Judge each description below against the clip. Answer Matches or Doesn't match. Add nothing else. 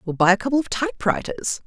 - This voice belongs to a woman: Matches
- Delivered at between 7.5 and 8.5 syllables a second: Matches